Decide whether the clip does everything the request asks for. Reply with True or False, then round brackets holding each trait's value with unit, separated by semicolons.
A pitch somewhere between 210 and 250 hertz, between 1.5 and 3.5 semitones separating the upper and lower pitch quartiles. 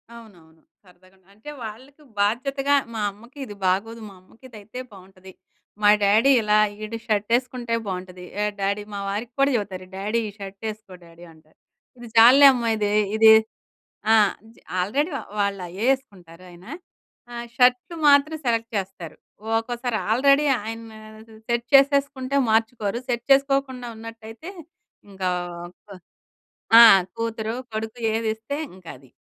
False (220 Hz; 3.9 semitones)